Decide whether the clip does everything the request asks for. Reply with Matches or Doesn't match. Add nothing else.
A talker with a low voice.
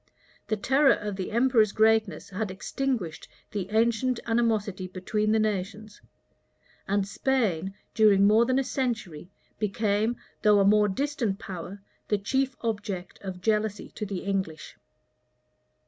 Doesn't match